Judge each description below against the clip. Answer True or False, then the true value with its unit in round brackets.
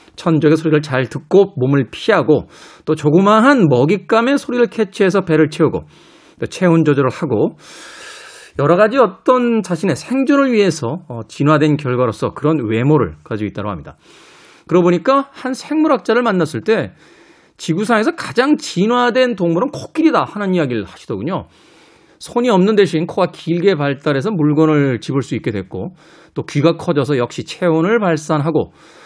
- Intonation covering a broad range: True (6.7 semitones)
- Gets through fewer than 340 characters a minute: True (330 characters per minute)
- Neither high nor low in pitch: True (165 Hz)